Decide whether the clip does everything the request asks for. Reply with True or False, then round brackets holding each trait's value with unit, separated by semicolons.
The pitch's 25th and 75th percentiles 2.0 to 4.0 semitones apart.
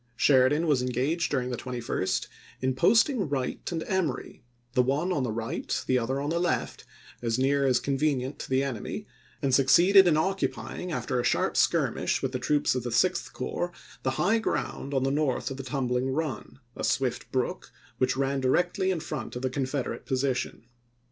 True (3.3 semitones)